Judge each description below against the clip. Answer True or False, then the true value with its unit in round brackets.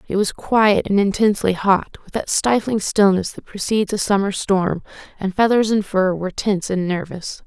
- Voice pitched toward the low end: False (200 Hz)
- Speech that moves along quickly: False (185 wpm)